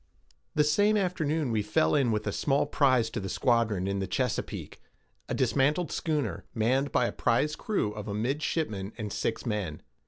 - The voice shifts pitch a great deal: Yes, wide, 5.9 semitones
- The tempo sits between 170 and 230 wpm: Yes, average, 180 wpm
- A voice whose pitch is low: Yes, low, 120 Hz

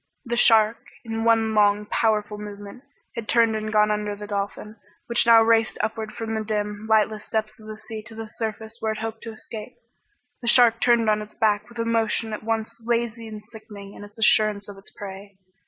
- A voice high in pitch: Yes, high, 220 Hz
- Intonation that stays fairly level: Yes, narrow, 1.2 semitones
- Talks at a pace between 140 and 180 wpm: No, fast, 205 wpm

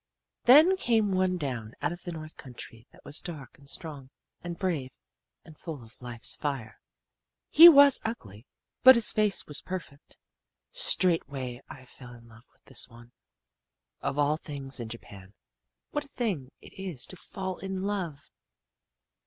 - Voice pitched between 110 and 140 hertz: No, medium, 150 Hz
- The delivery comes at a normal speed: Yes, average, 160 wpm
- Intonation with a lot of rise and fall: Yes, wide, 7.1 semitones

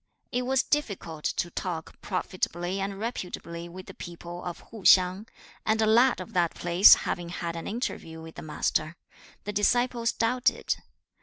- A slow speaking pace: No, average, 160 wpm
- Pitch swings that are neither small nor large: Yes, average, 4.6 semitones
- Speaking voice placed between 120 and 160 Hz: No, medium, 185 Hz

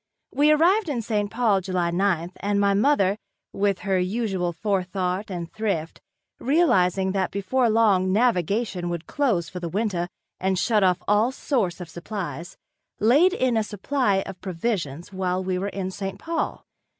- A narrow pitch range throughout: No, average, 3.7 semitones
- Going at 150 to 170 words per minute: Yes, average, 160 wpm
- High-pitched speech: Yes, high, 195 Hz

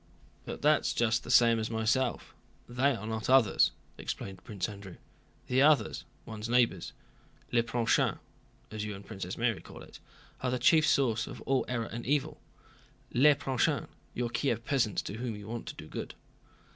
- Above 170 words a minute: No, average, 165 wpm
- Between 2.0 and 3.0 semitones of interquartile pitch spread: Yes, average, 2.7 semitones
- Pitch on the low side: Yes, low, 115 Hz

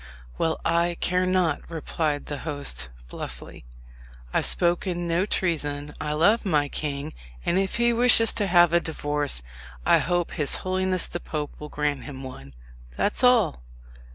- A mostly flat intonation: No, average, 4.0 semitones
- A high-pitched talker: No, medium, 165 Hz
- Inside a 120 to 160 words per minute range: Yes, average, 155 wpm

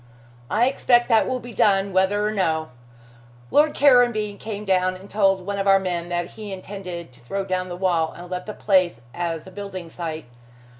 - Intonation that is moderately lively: Yes, average, 3.1 semitones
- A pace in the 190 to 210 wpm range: Yes, average, 195 wpm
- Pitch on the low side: No, high, 190 Hz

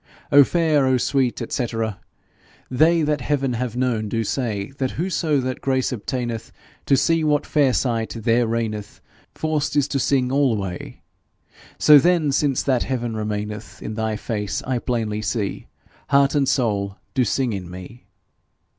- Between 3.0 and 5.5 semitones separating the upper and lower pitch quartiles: Yes, average, 4.2 semitones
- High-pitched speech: No, low, 125 Hz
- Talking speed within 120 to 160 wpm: Yes, average, 155 wpm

